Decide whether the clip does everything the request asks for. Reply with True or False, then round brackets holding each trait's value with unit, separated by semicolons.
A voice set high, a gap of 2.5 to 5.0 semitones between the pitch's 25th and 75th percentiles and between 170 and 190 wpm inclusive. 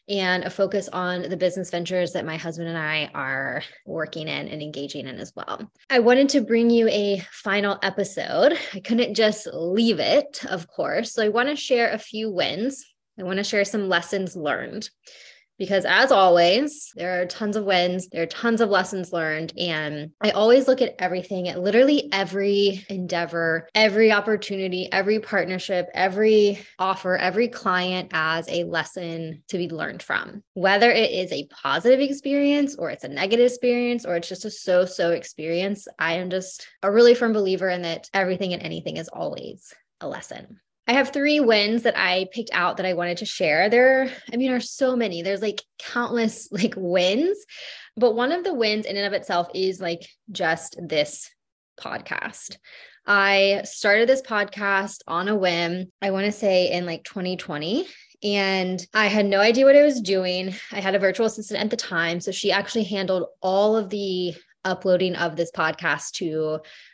True (195 Hz; 3.8 semitones; 185 wpm)